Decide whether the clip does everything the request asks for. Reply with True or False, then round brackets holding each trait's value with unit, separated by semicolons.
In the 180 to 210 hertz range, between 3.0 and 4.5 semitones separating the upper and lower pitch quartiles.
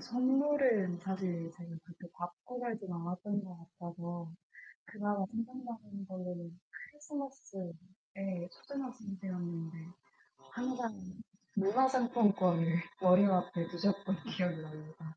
False (190 Hz; 5.3 semitones)